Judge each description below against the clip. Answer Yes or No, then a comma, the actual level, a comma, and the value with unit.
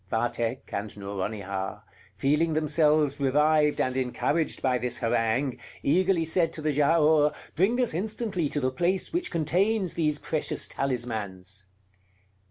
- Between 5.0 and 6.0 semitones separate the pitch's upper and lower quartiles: Yes, wide, 5.5 semitones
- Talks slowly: Yes, slow, 130 wpm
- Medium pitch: Yes, medium, 150 Hz